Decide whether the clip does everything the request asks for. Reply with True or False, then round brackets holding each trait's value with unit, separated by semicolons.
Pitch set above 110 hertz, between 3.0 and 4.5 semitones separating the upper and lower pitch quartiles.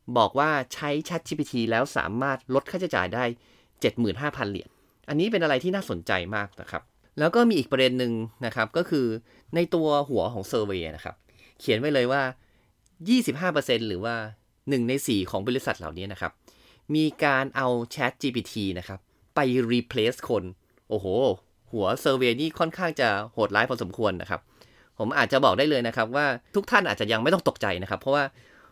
False (125 Hz; 5.4 semitones)